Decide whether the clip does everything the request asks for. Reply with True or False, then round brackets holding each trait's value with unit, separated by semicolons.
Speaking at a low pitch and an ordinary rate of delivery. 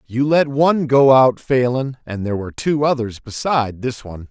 True (130 Hz; 195 wpm)